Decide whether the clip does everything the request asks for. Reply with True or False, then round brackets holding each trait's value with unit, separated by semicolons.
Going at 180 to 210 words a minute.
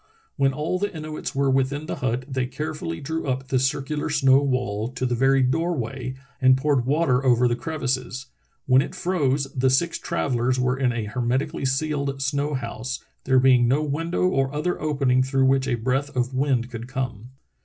True (185 wpm)